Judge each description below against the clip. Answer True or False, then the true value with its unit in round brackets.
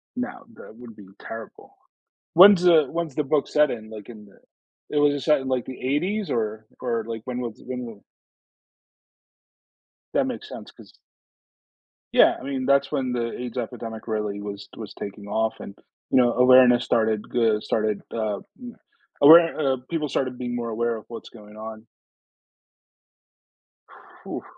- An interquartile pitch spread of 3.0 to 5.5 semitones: True (4.0 semitones)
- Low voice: True (120 Hz)